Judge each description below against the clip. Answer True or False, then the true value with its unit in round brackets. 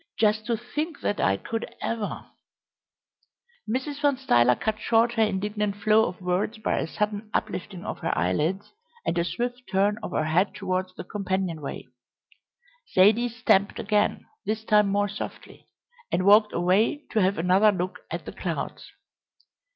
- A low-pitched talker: False (210 Hz)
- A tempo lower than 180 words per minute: True (160 wpm)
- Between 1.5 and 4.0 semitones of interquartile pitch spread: True (3.3 semitones)